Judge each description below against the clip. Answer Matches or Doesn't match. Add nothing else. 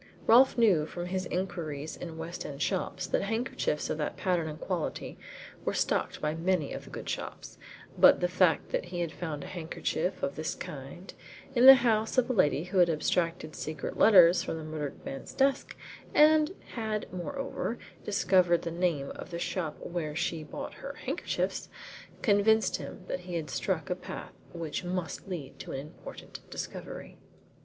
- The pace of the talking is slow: Doesn't match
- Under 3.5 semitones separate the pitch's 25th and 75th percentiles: Doesn't match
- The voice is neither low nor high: Matches